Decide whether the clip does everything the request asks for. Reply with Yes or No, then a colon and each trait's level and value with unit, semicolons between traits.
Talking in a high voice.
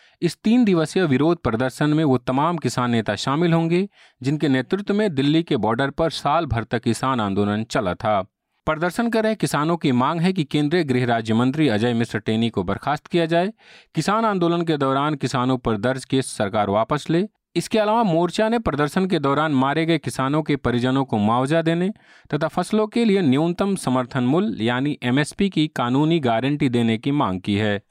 No: medium, 150 Hz